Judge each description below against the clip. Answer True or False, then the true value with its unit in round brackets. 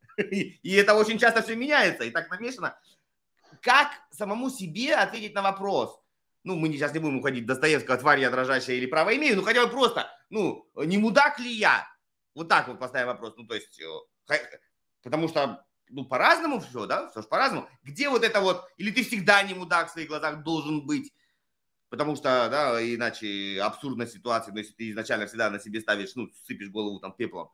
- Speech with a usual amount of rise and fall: False (9.0 semitones)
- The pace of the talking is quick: True (195 wpm)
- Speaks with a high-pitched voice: False (165 Hz)